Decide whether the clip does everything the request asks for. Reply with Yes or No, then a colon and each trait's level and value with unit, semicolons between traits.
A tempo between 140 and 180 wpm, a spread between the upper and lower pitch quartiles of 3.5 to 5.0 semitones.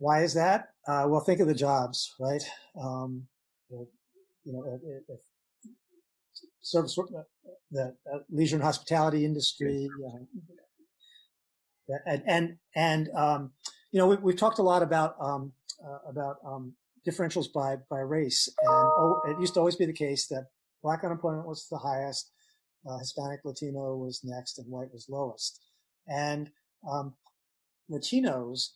Yes: average, 150 wpm; average, 4.4 semitones